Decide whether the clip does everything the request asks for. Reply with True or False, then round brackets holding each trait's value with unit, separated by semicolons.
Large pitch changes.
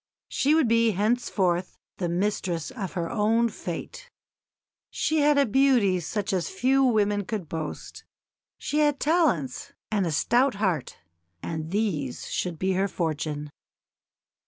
True (6.0 semitones)